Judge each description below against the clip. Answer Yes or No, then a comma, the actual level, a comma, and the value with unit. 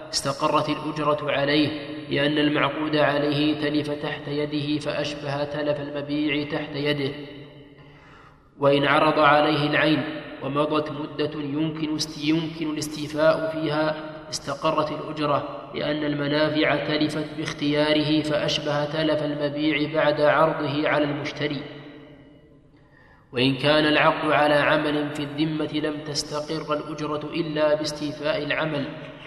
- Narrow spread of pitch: Yes, narrow, 0.8 semitones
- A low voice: No, medium, 150 Hz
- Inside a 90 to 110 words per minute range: Yes, average, 100 wpm